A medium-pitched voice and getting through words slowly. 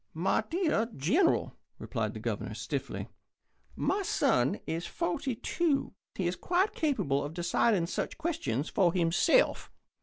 No: high, 220 Hz; slow, 130 wpm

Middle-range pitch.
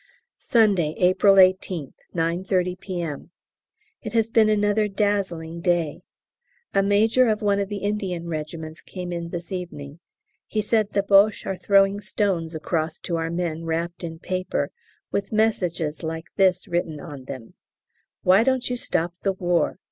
Yes: medium, 180 Hz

